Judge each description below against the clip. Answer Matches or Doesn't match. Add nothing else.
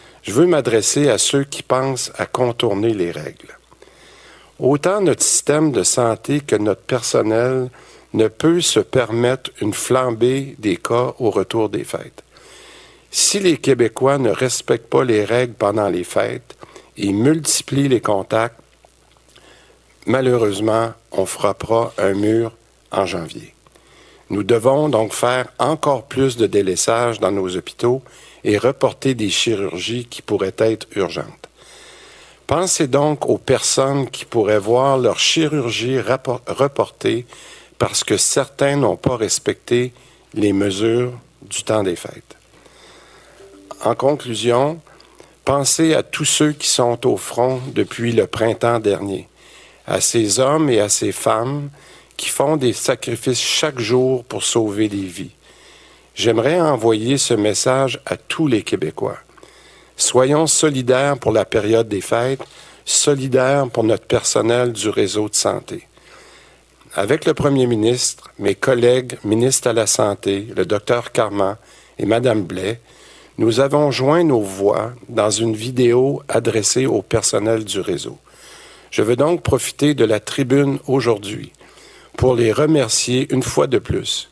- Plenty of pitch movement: Doesn't match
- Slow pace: Matches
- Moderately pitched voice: Doesn't match